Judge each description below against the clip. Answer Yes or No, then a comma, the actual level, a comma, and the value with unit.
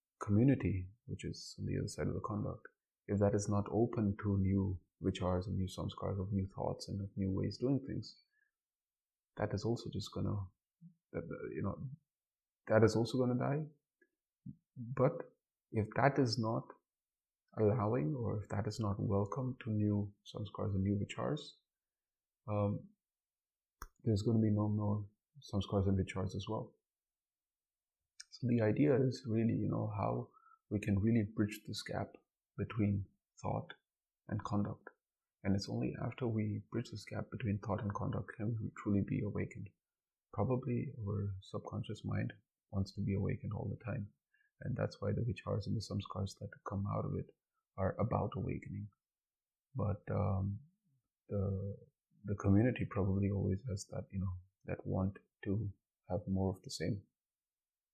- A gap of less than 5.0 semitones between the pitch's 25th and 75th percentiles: Yes, average, 3.2 semitones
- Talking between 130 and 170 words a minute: Yes, average, 160 wpm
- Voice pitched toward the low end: Yes, low, 105 Hz